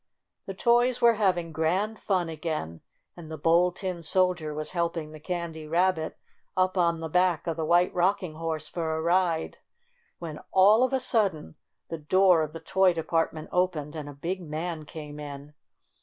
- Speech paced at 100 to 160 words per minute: No, average, 175 wpm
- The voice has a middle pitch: Yes, medium, 170 Hz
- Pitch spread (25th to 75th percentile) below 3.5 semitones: Yes, average, 2.9 semitones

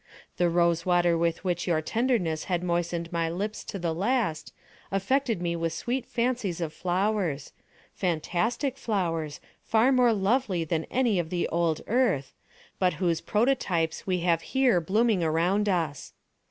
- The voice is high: No, medium, 180 Hz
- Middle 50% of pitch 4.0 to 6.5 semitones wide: Yes, average, 4.8 semitones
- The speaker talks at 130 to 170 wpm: Yes, average, 145 wpm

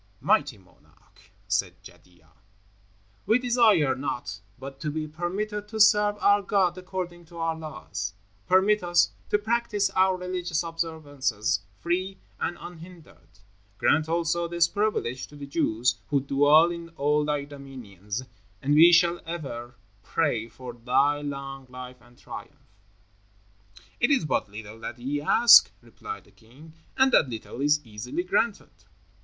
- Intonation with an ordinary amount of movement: No, wide, 5.8 semitones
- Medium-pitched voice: Yes, medium, 155 Hz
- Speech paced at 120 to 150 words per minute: Yes, average, 140 wpm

